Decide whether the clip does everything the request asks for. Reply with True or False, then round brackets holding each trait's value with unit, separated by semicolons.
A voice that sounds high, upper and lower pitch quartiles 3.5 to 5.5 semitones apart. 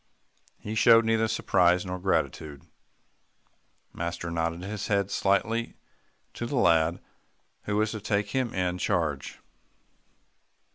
False (95 Hz; 4.2 semitones)